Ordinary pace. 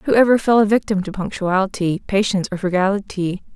Yes: average, 170 wpm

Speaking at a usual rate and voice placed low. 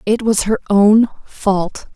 No: average, 155 wpm; high, 210 Hz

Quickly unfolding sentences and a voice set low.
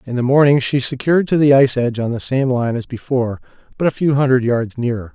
Yes: fast, 245 wpm; low, 130 Hz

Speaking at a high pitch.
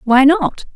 Yes: very high, 280 Hz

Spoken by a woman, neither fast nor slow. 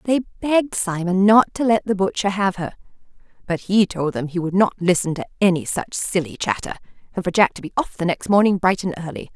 No: female; fast, 225 wpm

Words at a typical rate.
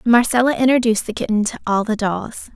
Yes: average, 190 wpm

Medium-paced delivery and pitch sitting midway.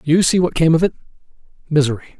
Yes: average, 165 wpm; medium, 160 Hz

